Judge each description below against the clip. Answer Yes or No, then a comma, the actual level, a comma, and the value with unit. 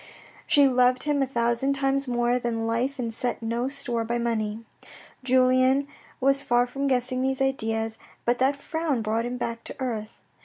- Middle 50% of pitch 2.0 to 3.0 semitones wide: Yes, narrow, 2.5 semitones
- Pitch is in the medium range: No, very high, 250 Hz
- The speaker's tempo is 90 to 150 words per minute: No, average, 170 wpm